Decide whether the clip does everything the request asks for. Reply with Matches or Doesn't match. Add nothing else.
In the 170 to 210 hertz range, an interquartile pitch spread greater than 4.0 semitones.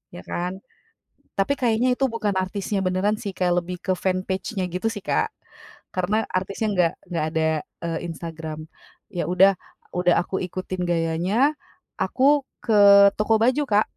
Doesn't match